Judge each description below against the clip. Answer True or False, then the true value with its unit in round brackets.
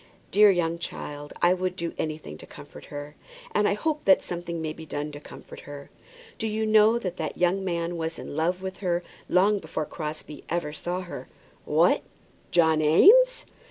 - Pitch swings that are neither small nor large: True (3.6 semitones)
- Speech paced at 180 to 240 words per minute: True (185 wpm)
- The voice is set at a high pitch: False (175 Hz)